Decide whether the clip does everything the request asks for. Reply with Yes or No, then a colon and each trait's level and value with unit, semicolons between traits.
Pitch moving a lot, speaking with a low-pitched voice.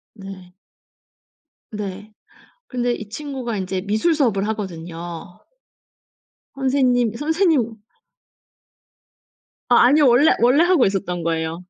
No: wide, 5.8 semitones; high, 220 Hz